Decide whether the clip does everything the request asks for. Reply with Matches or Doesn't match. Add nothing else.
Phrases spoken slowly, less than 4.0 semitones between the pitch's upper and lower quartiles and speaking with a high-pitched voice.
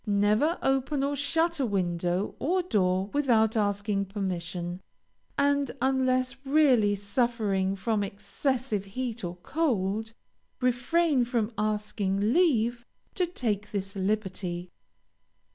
Doesn't match